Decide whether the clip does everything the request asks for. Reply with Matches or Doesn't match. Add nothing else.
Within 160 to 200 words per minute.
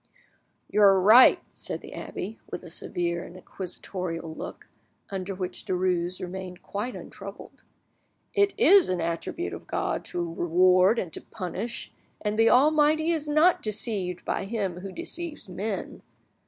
Doesn't match